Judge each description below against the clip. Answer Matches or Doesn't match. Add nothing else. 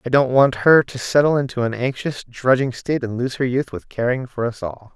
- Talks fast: Matches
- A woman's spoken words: Doesn't match